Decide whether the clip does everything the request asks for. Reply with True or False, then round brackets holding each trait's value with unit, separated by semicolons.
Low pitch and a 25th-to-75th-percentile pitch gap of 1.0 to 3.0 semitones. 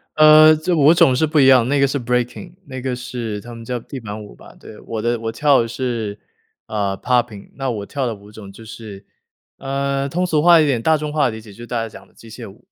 False (125 Hz; 4.0 semitones)